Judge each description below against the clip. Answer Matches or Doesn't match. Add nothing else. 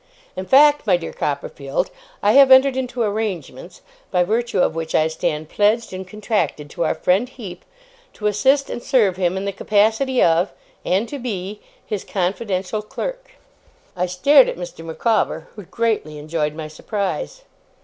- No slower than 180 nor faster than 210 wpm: Doesn't match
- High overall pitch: Matches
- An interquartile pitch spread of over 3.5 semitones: Matches